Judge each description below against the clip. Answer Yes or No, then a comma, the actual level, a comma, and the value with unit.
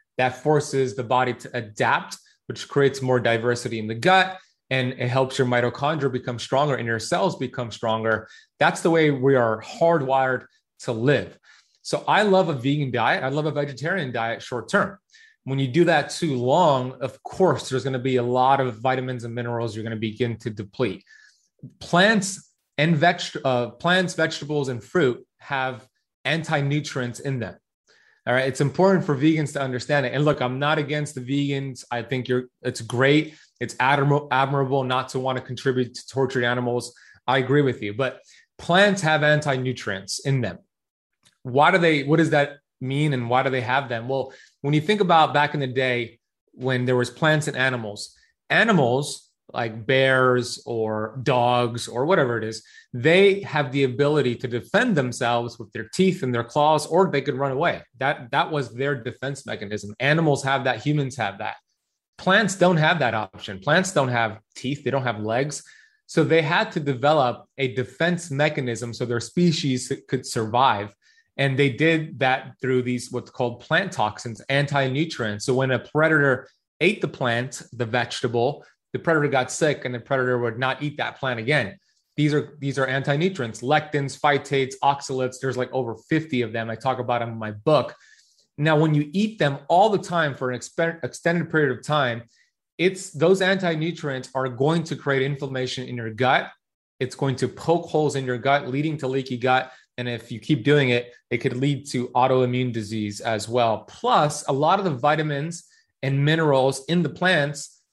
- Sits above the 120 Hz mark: Yes, low, 135 Hz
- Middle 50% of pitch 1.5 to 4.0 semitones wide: Yes, average, 3.4 semitones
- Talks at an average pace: Yes, average, 185 wpm